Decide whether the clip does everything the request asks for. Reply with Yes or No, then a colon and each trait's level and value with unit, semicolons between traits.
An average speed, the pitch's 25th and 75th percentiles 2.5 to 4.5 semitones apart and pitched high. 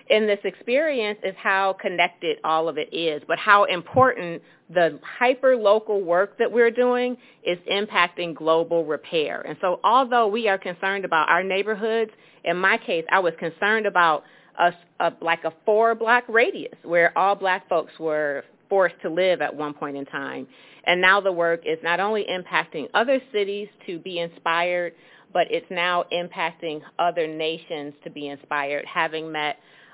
No: average, 170 wpm; average, 4.0 semitones; medium, 175 Hz